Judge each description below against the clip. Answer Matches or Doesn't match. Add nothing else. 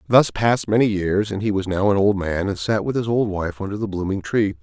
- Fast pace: Matches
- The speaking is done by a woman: Doesn't match